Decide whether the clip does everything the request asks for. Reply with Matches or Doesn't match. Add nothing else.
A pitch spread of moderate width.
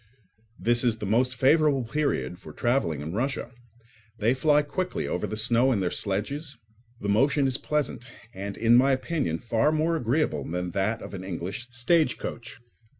Doesn't match